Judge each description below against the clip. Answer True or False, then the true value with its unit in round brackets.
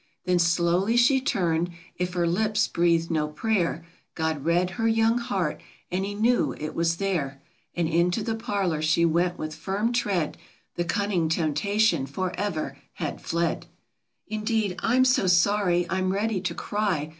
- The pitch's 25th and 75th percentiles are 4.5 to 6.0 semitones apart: False (3.9 semitones)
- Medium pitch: True (180 Hz)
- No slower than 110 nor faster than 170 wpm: True (155 wpm)